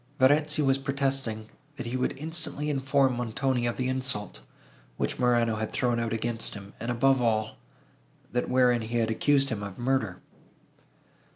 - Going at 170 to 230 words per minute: No, average, 160 wpm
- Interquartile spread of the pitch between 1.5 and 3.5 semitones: Yes, average, 3.1 semitones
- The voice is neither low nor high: No, low, 125 Hz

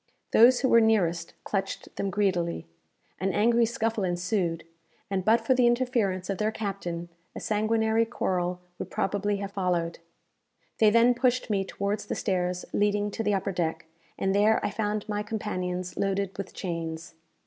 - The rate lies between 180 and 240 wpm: No, average, 160 wpm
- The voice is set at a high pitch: Yes, high, 200 Hz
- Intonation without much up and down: No, average, 3.4 semitones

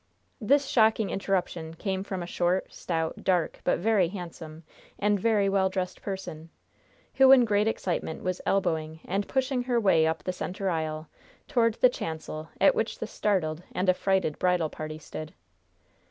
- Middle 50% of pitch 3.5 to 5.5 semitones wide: Yes, average, 4.3 semitones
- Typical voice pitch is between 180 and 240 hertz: Yes, medium, 185 Hz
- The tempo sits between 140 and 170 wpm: Yes, average, 160 wpm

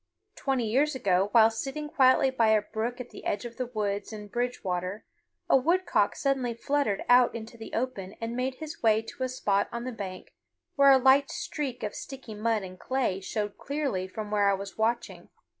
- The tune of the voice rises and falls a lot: No, average, 4.0 semitones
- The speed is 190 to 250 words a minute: Yes, average, 195 wpm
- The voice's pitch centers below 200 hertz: No, high, 235 Hz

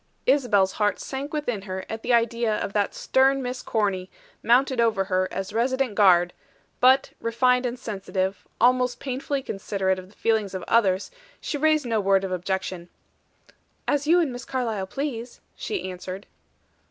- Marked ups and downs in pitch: No, average, 4.9 semitones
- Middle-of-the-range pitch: No, high, 225 Hz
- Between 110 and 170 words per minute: Yes, average, 160 wpm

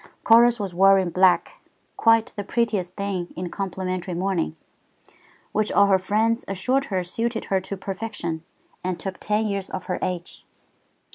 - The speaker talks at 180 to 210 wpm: No, average, 150 wpm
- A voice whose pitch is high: Yes, high, 195 Hz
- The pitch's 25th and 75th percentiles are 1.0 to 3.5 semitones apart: Yes, average, 2.9 semitones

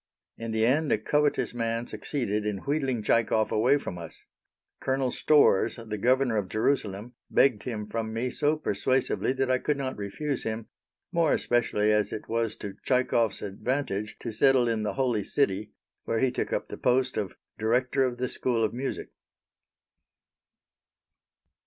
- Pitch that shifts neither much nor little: Yes, average, 3.6 semitones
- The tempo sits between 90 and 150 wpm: No, average, 160 wpm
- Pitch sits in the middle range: No, low, 115 Hz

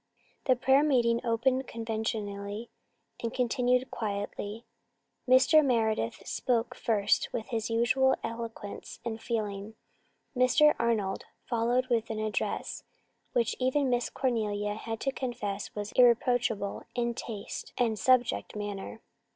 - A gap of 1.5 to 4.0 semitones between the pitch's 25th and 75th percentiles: Yes, average, 2.7 semitones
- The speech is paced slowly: Yes, slow, 120 wpm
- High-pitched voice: Yes, high, 230 Hz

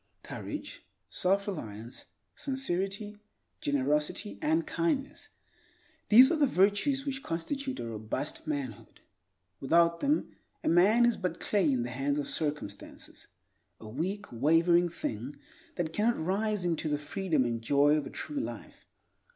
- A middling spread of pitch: No, wide, 8.6 semitones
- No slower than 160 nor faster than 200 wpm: No, slow, 135 wpm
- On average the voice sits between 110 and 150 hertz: No, medium, 175 Hz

